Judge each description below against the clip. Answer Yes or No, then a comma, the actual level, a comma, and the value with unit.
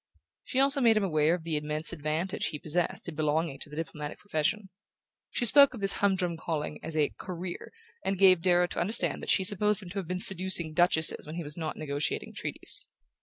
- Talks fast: Yes, fast, 210 wpm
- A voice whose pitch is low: No, medium, 175 Hz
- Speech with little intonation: No, average, 3.8 semitones